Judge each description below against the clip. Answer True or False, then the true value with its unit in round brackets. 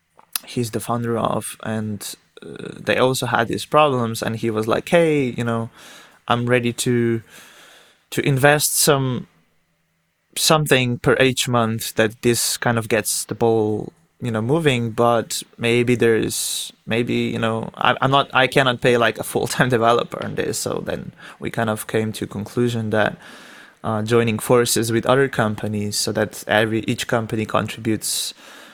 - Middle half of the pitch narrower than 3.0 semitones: True (2.6 semitones)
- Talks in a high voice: False (120 Hz)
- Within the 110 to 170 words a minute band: True (165 wpm)